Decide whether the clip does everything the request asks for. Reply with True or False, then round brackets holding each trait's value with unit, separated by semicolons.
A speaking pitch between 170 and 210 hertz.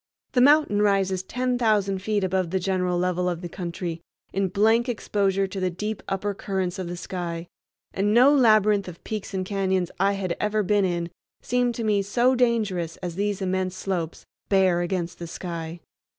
True (190 Hz)